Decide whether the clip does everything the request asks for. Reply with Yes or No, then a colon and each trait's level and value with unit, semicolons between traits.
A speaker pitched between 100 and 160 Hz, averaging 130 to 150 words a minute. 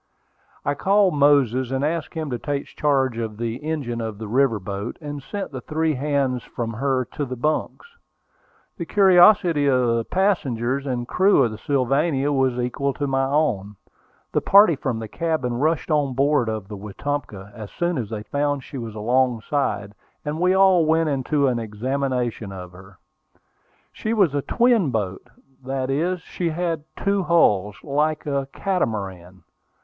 No: low, 135 Hz; average, 165 wpm